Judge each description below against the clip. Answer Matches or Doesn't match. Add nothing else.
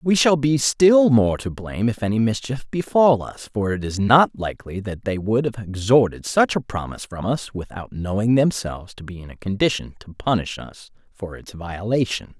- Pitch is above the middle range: Doesn't match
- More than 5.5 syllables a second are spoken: Doesn't match